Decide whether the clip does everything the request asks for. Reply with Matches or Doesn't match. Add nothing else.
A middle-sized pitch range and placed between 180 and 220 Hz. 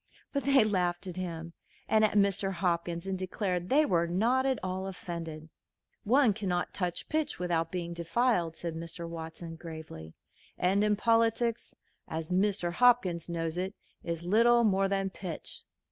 Matches